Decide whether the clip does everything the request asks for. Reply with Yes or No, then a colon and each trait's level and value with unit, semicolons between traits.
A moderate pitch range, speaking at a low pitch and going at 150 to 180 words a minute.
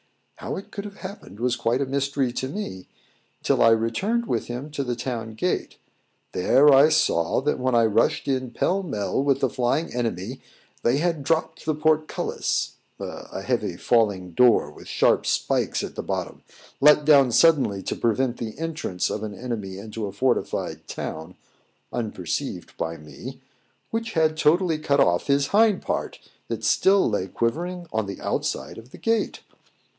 No: wide, 5.9 semitones; low, 130 Hz; average, 170 wpm